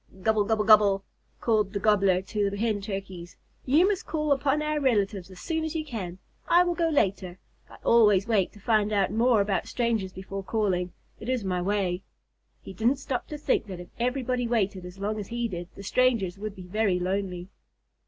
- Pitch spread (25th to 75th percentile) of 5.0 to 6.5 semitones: No, average, 4.0 semitones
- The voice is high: Yes, high, 210 Hz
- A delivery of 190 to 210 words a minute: Yes, average, 200 wpm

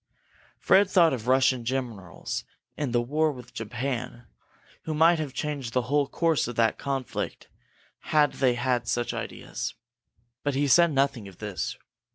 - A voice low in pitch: Yes, low, 130 Hz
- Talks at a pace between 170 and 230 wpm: No, average, 155 wpm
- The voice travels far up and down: No, average, 3.5 semitones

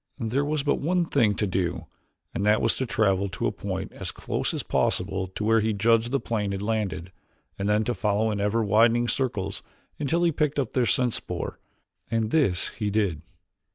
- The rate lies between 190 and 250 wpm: Yes, average, 200 wpm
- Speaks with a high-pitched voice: No, low, 110 Hz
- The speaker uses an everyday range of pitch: Yes, average, 3.6 semitones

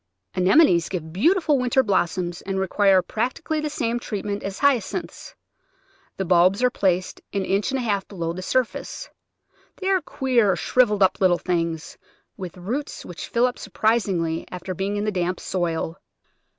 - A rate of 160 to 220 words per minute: Yes, average, 165 wpm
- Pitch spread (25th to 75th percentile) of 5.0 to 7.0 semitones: Yes, average, 5.3 semitones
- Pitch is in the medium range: No, high, 195 Hz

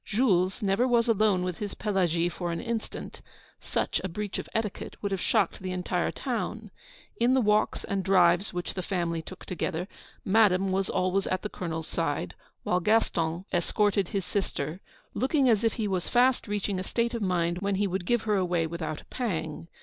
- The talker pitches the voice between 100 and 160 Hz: No, high, 190 Hz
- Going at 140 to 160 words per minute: No, average, 190 wpm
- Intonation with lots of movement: No, average, 3.4 semitones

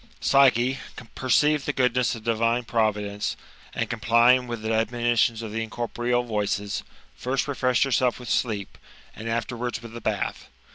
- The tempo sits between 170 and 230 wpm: No, average, 145 wpm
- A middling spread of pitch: No, narrow, 2.0 semitones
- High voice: No, low, 120 Hz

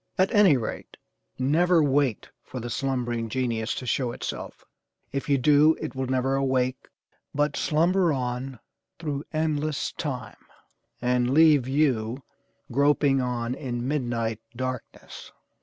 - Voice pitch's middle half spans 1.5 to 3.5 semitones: Yes, average, 3.1 semitones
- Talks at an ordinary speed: No, slow, 125 wpm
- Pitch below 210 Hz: Yes, low, 135 Hz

